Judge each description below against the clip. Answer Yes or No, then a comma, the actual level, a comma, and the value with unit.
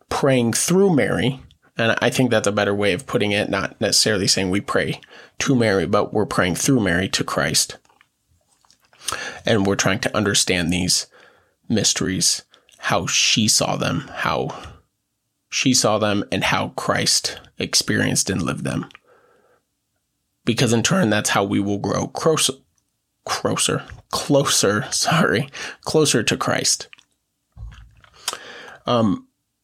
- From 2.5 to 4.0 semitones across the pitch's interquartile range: No, average, 4.5 semitones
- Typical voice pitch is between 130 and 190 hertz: No, low, 115 Hz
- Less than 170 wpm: Yes, slow, 135 wpm